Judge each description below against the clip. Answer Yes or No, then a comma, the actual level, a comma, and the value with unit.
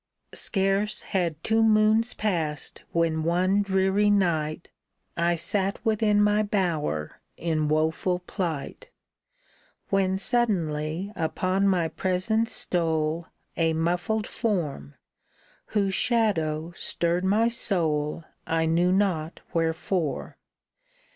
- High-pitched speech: No, medium, 180 Hz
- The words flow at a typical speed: No, slow, 100 wpm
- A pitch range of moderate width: Yes, average, 4.1 semitones